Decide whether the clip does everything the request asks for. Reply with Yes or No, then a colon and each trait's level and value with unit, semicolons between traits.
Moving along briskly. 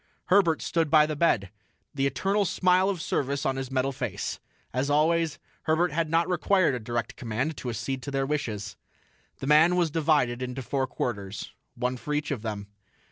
No: average, 185 wpm